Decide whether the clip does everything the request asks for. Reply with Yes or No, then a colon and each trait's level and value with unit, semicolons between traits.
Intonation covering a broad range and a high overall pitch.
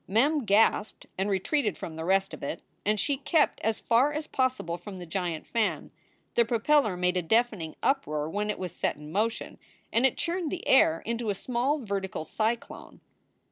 Yes: wide, 6.0 semitones; high, 215 Hz